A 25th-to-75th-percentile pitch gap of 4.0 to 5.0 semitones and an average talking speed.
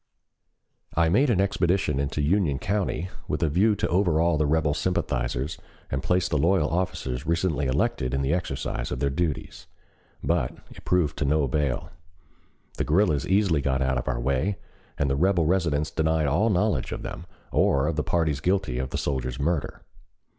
Yes: average, 4.6 semitones; average, 175 wpm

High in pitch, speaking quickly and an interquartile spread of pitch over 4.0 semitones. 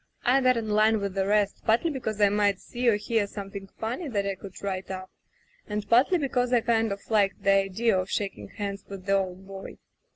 No: high, 205 Hz; fast, 220 wpm; average, 2.7 semitones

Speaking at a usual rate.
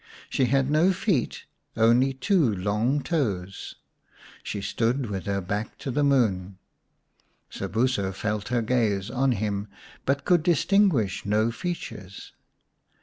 No: slow, 125 wpm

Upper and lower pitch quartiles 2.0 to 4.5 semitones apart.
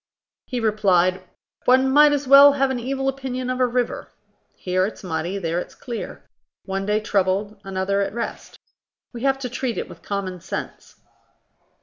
No: wide, 5.4 semitones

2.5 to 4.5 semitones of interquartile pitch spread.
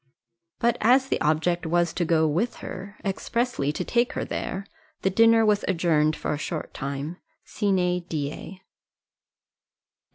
No: average, 5.0 semitones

